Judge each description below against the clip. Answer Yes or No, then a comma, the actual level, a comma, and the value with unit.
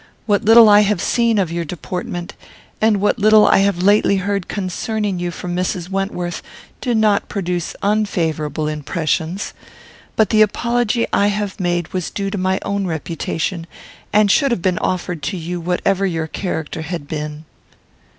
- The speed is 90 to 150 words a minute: No, average, 160 wpm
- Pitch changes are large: No, average, 3.3 semitones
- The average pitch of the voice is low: No, medium, 185 Hz